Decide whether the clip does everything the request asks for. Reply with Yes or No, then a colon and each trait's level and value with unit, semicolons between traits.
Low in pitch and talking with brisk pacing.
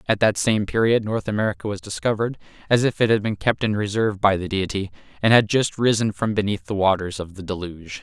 Yes: low, 105 Hz; fast, 225 wpm